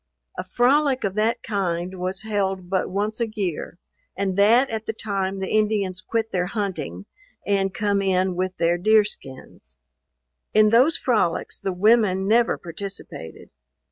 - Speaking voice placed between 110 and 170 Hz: No, high, 200 Hz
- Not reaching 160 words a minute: Yes, average, 150 wpm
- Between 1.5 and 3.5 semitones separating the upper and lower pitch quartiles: Yes, average, 2.7 semitones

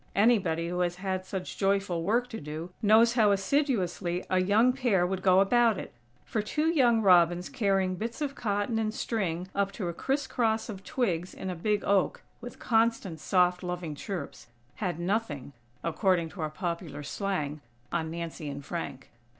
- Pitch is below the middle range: No, high, 190 Hz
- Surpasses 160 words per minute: Yes, average, 175 wpm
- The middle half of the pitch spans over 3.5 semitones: Yes, average, 4.4 semitones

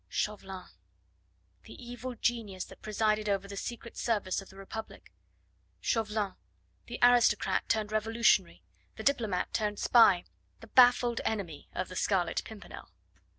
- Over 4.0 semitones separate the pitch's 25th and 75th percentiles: No, average, 3.1 semitones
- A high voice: Yes, high, 215 Hz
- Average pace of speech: No, slow, 130 wpm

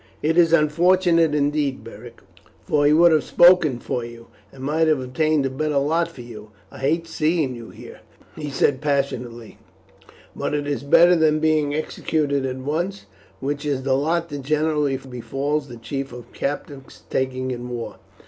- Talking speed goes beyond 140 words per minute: Yes, average, 170 wpm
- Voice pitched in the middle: Yes, medium, 145 Hz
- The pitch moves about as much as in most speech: Yes, average, 3.0 semitones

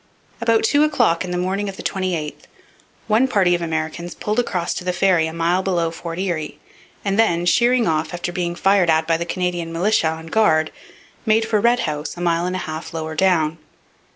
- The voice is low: No, medium, 175 Hz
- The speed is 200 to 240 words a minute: Yes, fast, 205 wpm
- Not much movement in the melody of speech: No, average, 3.3 semitones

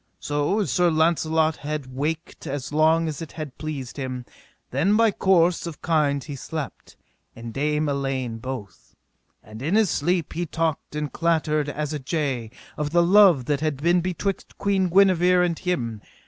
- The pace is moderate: Yes, average, 170 wpm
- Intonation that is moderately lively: Yes, average, 3.6 semitones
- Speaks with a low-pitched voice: No, medium, 155 Hz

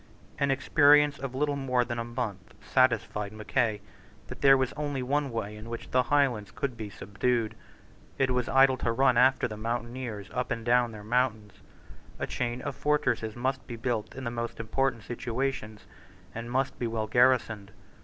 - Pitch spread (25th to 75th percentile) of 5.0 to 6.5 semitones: No, average, 3.0 semitones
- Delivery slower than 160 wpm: No, average, 175 wpm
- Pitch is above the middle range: No, low, 120 Hz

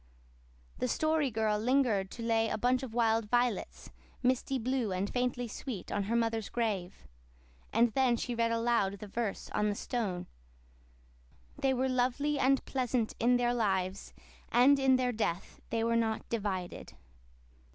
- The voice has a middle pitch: No, high, 230 Hz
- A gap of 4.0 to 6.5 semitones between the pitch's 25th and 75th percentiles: No, average, 3.0 semitones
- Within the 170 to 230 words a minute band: No, average, 155 wpm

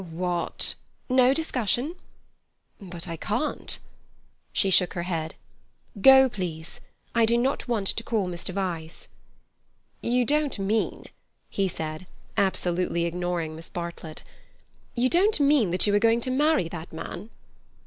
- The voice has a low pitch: No, high, 195 Hz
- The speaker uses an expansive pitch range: Yes, wide, 6.2 semitones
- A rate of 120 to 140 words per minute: Yes, slow, 135 wpm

